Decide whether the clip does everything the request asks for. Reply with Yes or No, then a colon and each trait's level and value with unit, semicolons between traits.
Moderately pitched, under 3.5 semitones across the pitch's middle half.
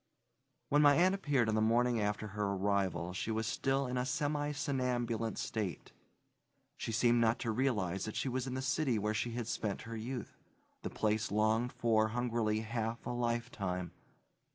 No: low, 115 Hz; average, 2.7 semitones